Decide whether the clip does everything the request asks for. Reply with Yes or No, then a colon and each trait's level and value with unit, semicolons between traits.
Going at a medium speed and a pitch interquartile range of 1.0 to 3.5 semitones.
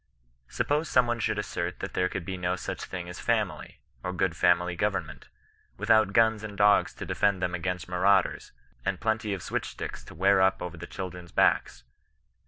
Yes: average, 190 wpm; narrow, 2.5 semitones